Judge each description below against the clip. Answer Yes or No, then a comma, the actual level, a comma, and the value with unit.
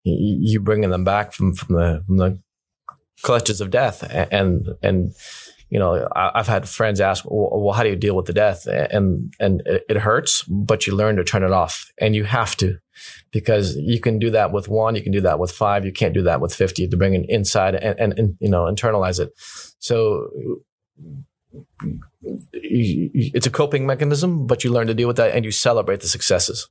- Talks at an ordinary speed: No, fast, 210 wpm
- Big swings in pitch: No, average, 3.6 semitones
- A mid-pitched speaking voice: No, low, 105 Hz